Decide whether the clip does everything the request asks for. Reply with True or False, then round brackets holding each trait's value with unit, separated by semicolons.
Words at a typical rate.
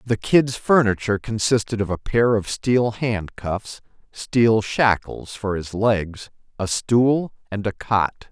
True (150 wpm)